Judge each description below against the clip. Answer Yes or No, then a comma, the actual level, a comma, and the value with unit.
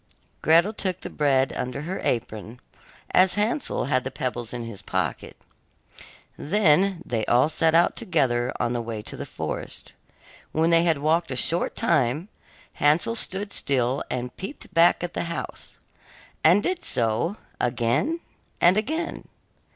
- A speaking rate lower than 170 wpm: Yes, average, 150 wpm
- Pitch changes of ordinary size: No, wide, 6.8 semitones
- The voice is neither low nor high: Yes, medium, 155 Hz